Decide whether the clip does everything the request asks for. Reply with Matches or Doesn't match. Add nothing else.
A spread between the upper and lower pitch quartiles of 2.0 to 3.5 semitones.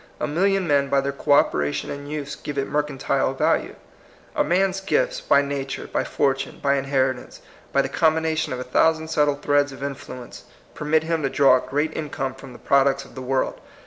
Matches